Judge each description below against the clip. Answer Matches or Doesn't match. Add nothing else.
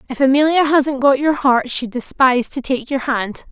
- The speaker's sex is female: Matches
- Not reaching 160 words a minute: Doesn't match